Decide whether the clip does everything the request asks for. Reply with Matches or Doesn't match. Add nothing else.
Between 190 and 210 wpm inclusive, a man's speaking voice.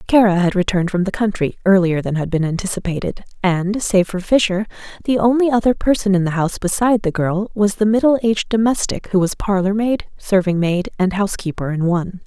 Doesn't match